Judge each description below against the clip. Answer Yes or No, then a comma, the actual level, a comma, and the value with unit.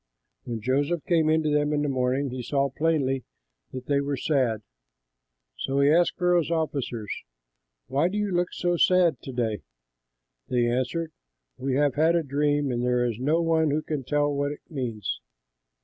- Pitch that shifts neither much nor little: Yes, average, 3.8 semitones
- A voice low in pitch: No, medium, 145 Hz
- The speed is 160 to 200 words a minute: Yes, average, 180 wpm